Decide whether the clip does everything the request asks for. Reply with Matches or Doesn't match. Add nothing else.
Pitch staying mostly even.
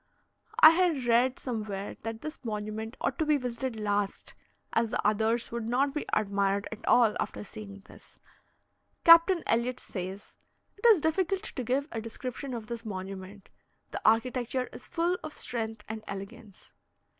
Doesn't match